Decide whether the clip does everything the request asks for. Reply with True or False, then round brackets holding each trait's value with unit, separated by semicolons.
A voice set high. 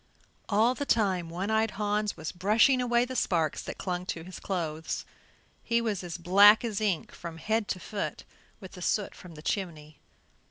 True (195 Hz)